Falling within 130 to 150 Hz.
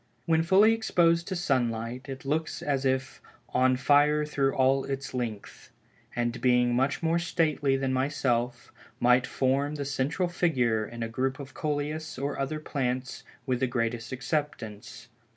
Yes: low, 135 Hz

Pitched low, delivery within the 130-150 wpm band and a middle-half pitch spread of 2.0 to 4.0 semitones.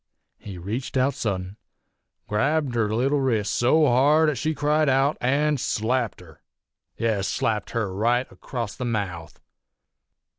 No: low, 120 Hz; average, 140 wpm; average, 4.8 semitones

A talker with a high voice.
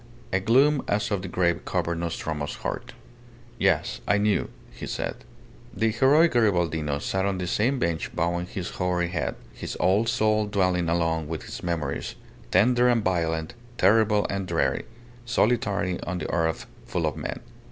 No: very low, 95 Hz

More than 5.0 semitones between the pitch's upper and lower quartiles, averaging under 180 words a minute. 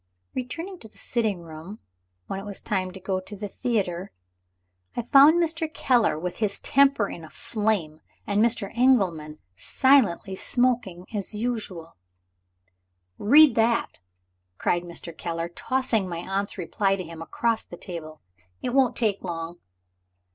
Yes: wide, 5.6 semitones; average, 145 wpm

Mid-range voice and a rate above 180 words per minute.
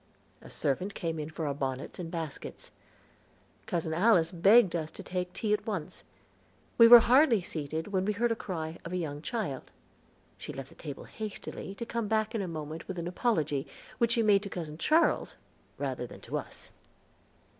Yes: medium, 180 Hz; average, 190 wpm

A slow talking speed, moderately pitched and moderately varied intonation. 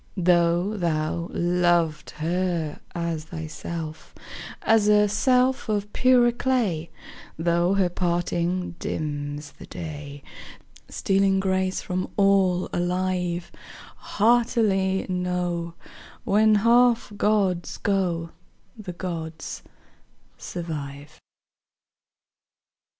Yes: slow, 85 wpm; medium, 180 Hz; average, 3.0 semitones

